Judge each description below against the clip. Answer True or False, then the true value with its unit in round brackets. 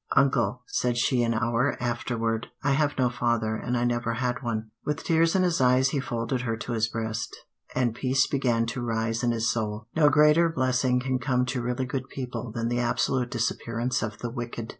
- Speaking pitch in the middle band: False (120 Hz)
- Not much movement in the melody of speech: True (2.0 semitones)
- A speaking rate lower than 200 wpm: False (205 wpm)